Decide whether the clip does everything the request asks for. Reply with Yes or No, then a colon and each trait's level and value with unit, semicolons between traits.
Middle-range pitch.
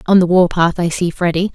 Yes: medium, 175 Hz